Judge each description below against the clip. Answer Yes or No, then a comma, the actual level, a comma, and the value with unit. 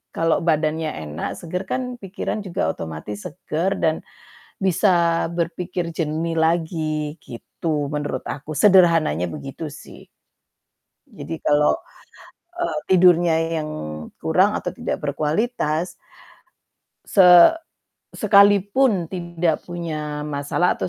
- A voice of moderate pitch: Yes, medium, 165 Hz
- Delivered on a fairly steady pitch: No, average, 3.2 semitones